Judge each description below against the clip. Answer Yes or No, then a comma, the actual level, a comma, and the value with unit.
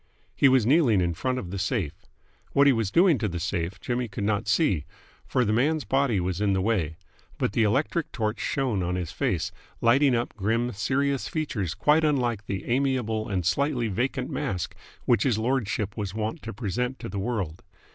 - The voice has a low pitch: Yes, low, 115 Hz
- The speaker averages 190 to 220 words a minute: Yes, average, 195 wpm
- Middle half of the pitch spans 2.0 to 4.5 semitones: No, average, 5.1 semitones